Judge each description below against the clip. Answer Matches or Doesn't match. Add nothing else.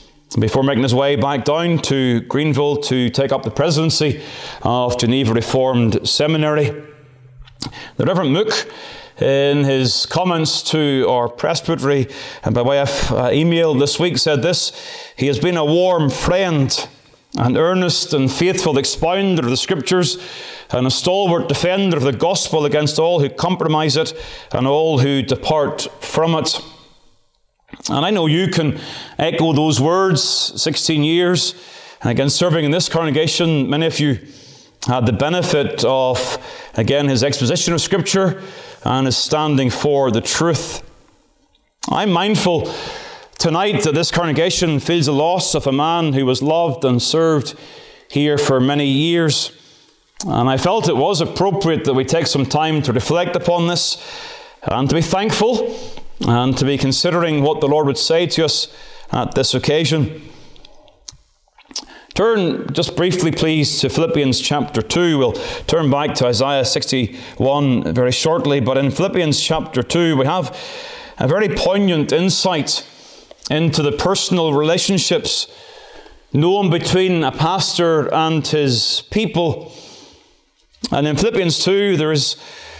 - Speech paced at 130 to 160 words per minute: Matches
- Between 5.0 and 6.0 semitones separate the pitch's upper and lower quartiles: Doesn't match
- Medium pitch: Matches